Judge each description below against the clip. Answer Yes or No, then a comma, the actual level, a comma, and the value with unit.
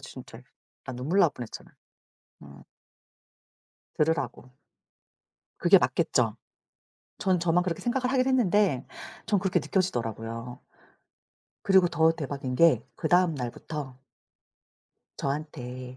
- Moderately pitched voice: Yes, medium, 155 Hz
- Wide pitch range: Yes, wide, 6.5 semitones